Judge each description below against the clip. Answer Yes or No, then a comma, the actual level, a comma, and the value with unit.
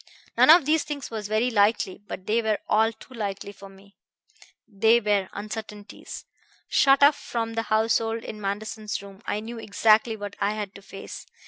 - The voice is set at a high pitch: Yes, high, 215 Hz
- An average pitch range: No, narrow, 2.0 semitones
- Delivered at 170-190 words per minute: Yes, average, 180 wpm